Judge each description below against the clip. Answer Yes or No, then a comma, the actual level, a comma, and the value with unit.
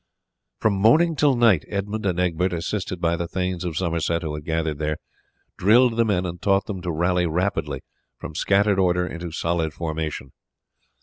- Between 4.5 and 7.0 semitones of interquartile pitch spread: No, average, 3.2 semitones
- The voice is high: No, very low, 90 Hz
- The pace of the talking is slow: No, average, 175 wpm